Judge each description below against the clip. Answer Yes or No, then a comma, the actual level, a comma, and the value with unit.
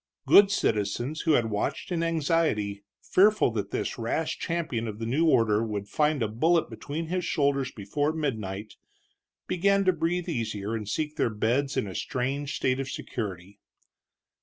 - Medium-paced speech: Yes, average, 160 wpm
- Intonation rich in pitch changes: Yes, wide, 7.1 semitones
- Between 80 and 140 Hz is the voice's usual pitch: Yes, low, 135 Hz